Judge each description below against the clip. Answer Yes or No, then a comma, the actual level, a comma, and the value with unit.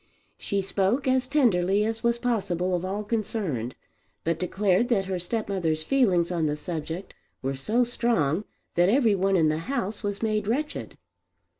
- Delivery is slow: No, average, 160 wpm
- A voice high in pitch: Yes, high, 195 Hz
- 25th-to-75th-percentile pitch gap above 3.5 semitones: Yes, average, 4.8 semitones